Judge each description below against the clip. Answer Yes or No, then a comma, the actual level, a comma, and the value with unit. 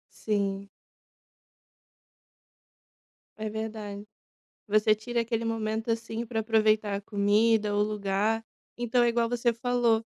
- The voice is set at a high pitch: Yes, high, 220 Hz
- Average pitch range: No, narrow, 1.7 semitones